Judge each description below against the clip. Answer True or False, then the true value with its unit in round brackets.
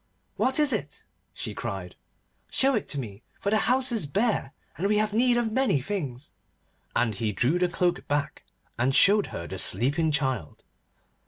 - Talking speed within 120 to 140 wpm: False (175 wpm)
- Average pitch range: False (9.0 semitones)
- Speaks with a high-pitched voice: False (165 Hz)